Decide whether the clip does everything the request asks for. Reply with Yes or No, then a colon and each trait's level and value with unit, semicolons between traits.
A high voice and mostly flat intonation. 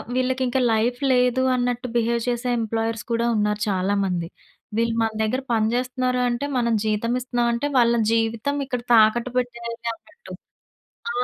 Yes: high, 235 Hz; narrow, 1.9 semitones